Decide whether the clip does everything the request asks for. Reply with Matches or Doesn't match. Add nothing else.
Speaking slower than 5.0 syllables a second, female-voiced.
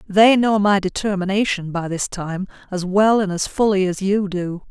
Matches